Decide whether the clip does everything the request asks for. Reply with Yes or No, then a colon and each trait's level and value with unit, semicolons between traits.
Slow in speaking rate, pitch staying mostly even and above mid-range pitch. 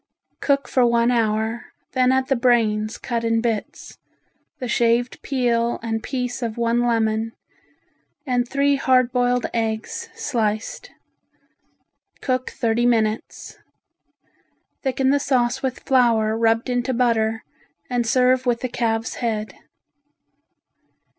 Yes: slow, 120 wpm; narrow, 2.0 semitones; high, 240 Hz